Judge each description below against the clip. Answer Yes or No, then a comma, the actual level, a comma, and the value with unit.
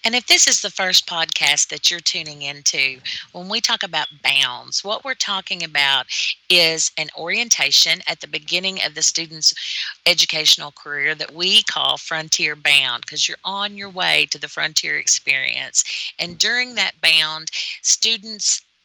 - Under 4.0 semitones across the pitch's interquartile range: No, average, 4.3 semitones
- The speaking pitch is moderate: Yes, medium, 165 Hz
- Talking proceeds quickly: No, average, 160 wpm